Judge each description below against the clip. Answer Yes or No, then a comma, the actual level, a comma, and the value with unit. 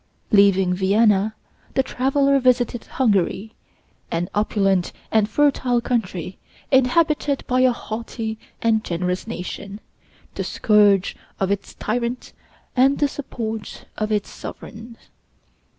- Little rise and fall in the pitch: No, average, 4.0 semitones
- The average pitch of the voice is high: Yes, high, 220 Hz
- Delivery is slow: Yes, slow, 110 wpm